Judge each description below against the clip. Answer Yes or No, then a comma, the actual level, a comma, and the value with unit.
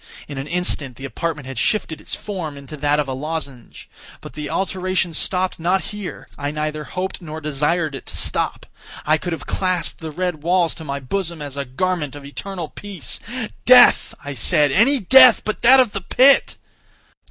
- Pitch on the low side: No, medium, 160 Hz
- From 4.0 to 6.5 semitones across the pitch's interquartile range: Yes, average, 4.4 semitones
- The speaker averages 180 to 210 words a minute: Yes, average, 185 wpm